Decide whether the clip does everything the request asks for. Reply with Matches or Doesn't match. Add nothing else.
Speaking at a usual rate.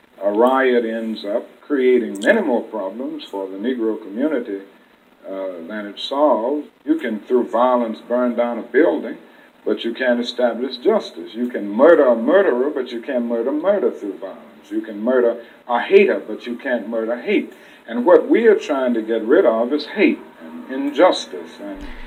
Matches